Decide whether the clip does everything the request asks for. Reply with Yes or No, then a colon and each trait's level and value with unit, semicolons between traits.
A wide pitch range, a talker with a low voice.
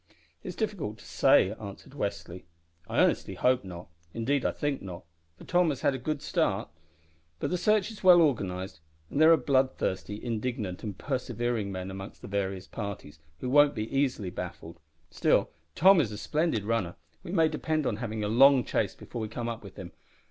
Yes: wide, 6.8 semitones; low, 115 Hz